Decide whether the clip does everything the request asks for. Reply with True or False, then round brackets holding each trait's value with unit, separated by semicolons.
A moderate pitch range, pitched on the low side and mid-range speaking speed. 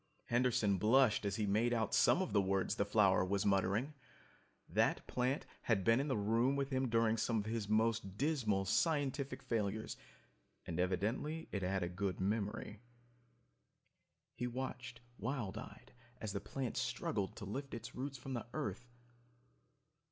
True (4.2 semitones; 110 Hz; 160 wpm)